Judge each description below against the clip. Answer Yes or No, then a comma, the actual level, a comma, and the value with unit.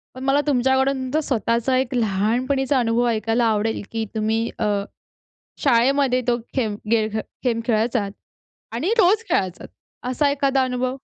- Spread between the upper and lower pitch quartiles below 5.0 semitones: Yes, average, 2.9 semitones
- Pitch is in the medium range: No, high, 245 Hz